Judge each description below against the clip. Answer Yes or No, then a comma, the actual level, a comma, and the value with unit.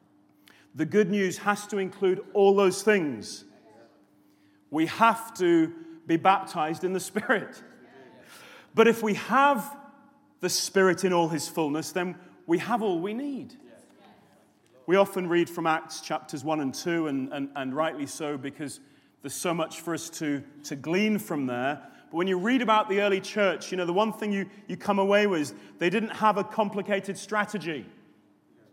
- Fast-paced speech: No, average, 175 wpm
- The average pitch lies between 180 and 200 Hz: Yes, medium, 185 Hz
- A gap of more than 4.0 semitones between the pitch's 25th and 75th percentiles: Yes, average, 4.5 semitones